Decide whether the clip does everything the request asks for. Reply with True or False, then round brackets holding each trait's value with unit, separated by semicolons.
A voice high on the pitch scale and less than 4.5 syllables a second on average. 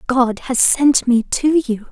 True (255 Hz; 3.6 syllables/s)